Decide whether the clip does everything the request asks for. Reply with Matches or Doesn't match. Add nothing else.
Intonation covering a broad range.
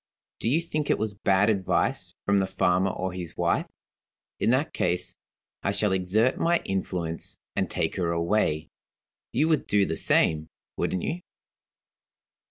Doesn't match